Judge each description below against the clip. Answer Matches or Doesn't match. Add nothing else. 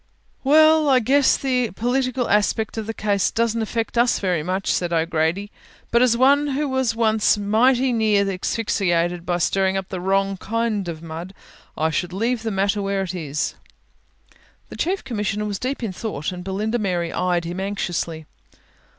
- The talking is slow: Doesn't match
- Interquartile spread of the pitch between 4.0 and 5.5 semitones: Matches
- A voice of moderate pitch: Doesn't match